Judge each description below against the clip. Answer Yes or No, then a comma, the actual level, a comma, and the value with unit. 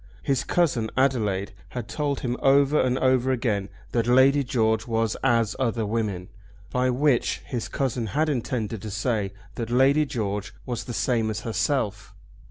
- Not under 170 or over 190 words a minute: No, average, 160 wpm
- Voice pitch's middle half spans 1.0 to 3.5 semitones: Yes, average, 3.2 semitones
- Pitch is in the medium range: No, low, 120 Hz